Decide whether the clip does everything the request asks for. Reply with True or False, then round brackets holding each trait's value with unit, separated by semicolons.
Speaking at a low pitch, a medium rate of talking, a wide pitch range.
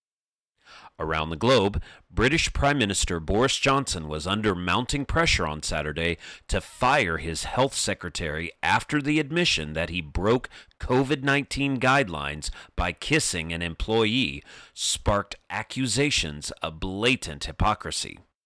False (95 Hz; 120 wpm; 8.6 semitones)